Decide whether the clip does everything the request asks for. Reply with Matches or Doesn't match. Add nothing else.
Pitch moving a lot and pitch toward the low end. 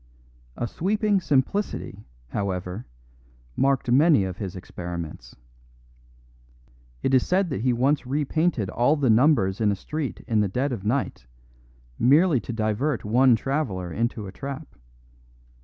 Matches